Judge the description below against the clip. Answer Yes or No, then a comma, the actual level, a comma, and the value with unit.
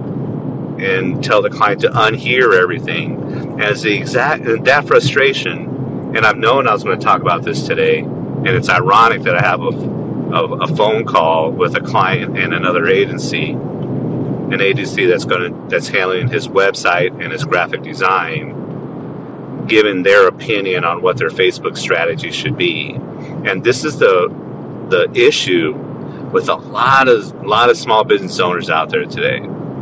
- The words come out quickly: No, average, 165 wpm